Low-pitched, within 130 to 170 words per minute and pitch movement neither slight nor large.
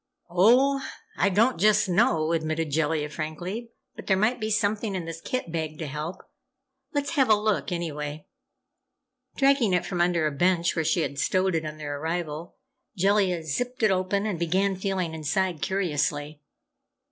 No: medium, 175 Hz; average, 165 wpm; average, 4.6 semitones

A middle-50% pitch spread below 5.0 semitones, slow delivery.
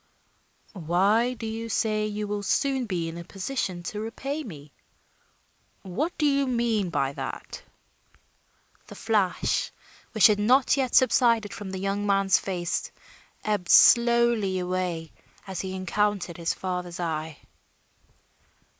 Yes: average, 4.3 semitones; slow, 130 wpm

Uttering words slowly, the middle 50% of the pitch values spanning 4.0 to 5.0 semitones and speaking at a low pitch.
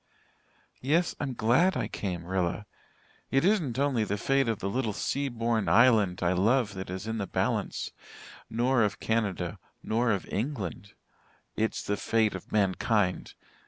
No: average, 155 wpm; average, 4.5 semitones; low, 110 Hz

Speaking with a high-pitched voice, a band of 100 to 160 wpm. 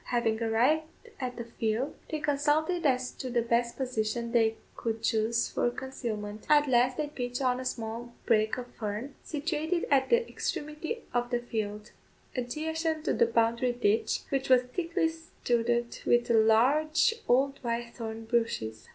Yes: high, 245 Hz; average, 155 wpm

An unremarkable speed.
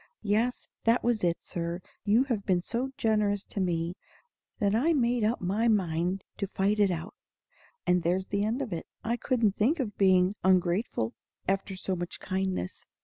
Yes: average, 175 wpm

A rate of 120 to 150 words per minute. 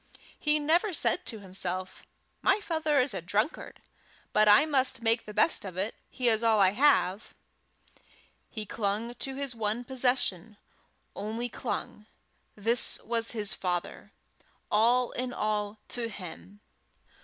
Yes: average, 140 wpm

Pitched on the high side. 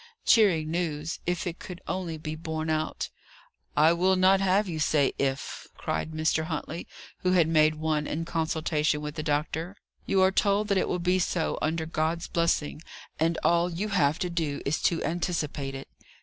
No: medium, 165 Hz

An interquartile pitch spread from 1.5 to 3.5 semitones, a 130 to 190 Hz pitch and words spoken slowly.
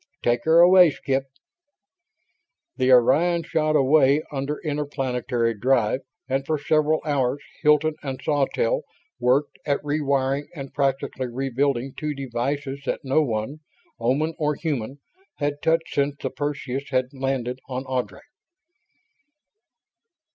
Yes: narrow, 2.4 semitones; medium, 140 Hz; slow, 125 wpm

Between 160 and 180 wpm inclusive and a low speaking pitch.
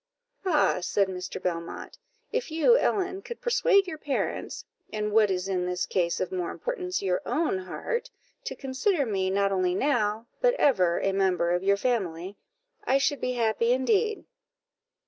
No: average, 165 wpm; high, 215 Hz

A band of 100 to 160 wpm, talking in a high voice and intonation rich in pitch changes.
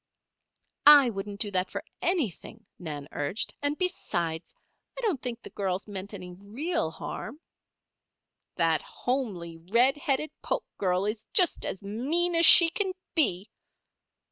Yes: average, 140 wpm; high, 215 Hz; wide, 8.3 semitones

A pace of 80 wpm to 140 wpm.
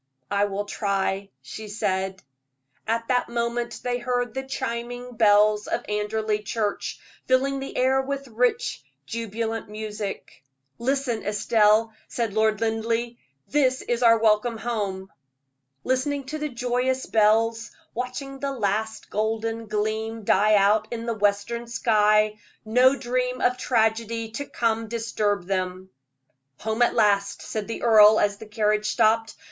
Yes: slow, 135 wpm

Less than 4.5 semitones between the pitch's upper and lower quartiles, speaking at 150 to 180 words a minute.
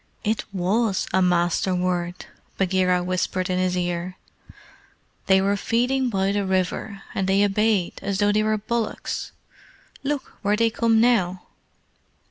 No: average, 2.9 semitones; average, 140 wpm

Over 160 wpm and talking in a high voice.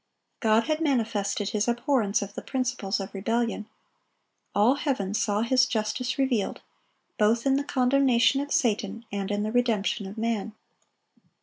No: average, 145 wpm; high, 230 Hz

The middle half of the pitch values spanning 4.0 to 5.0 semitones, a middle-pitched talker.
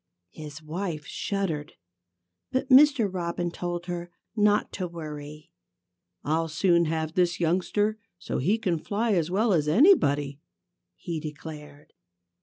Yes: average, 4.5 semitones; medium, 170 Hz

